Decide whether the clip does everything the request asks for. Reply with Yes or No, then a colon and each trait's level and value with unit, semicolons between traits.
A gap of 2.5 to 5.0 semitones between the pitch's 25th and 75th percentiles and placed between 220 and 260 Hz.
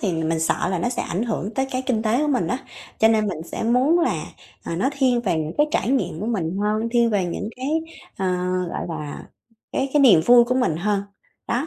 No: wide, 5.5 semitones; high, 225 Hz